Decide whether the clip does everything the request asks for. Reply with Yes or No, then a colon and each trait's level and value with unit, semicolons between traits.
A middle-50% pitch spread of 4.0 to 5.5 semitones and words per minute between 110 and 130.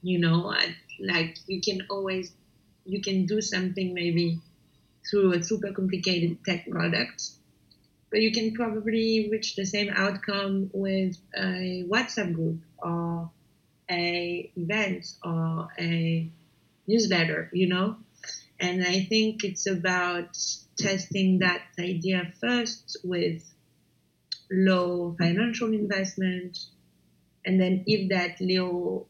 No: narrow, 2.6 semitones; slow, 115 wpm